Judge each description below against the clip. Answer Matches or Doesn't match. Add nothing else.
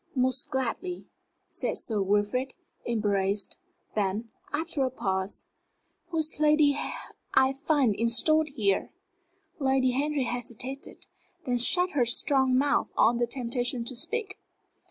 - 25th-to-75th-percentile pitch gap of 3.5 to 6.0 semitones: Matches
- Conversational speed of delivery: Doesn't match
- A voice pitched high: Matches